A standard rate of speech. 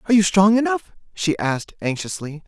Yes: average, 170 wpm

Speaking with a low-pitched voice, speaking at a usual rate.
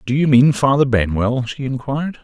Yes: low, 130 Hz; average, 190 wpm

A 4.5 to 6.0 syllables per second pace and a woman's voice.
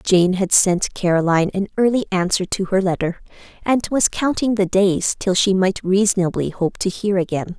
Yes: 4.9 syllables/s; female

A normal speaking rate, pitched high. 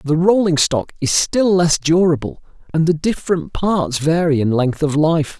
No: average, 180 wpm; medium, 160 Hz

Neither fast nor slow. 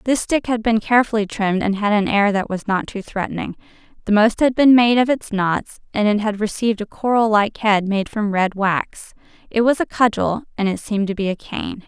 No: fast, 230 wpm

